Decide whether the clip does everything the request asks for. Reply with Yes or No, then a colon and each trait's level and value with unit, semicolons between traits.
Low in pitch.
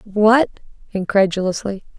No: high, 205 Hz